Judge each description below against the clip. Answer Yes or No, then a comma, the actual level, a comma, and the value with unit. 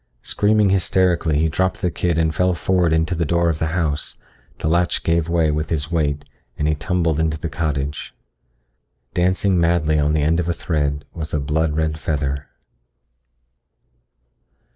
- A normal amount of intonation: No, narrow, 2.3 semitones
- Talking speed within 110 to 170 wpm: Yes, average, 165 wpm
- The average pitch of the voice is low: Yes, very low, 80 Hz